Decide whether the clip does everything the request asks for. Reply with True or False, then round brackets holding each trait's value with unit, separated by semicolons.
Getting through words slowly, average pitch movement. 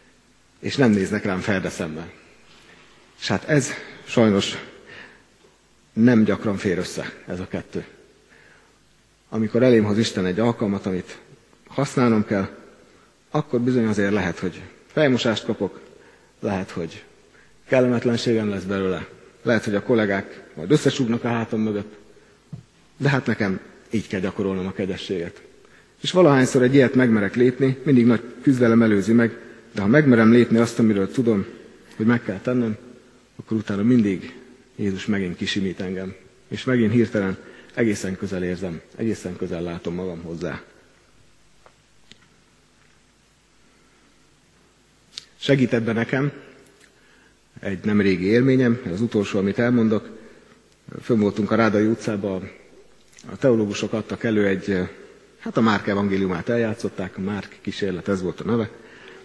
False (130 wpm; 3.5 semitones)